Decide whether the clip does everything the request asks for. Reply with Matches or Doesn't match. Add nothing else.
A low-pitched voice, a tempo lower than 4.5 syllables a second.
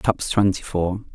Doesn't match